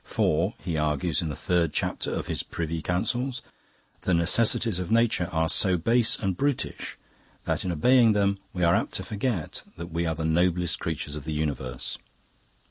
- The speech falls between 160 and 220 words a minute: Yes, average, 180 wpm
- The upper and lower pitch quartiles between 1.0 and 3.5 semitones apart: No, average, 4.3 semitones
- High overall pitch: No, very low, 85 Hz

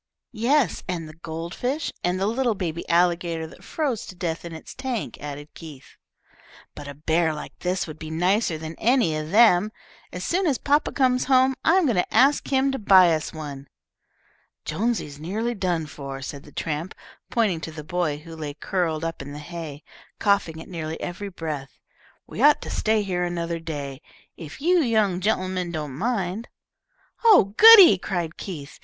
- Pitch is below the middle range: No, medium, 175 Hz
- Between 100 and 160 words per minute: No, average, 180 wpm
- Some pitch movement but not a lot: No, wide, 5.9 semitones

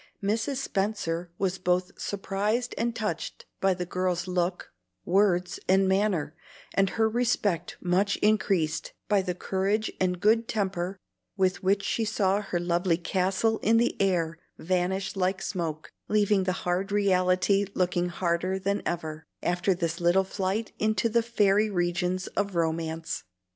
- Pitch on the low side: No, high, 190 Hz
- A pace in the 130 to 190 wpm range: Yes, average, 145 wpm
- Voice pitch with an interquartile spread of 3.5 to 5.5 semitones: No, narrow, 2.5 semitones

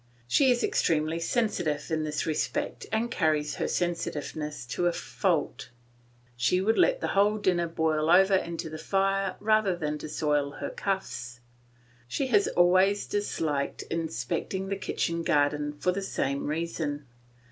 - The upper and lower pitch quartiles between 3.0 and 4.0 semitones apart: No, average, 4.4 semitones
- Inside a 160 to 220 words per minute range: No, average, 145 wpm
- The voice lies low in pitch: No, medium, 170 Hz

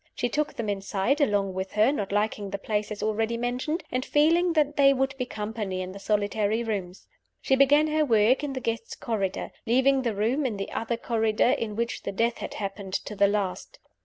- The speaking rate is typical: No, fast, 210 wpm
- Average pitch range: Yes, average, 4.6 semitones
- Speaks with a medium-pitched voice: No, high, 225 Hz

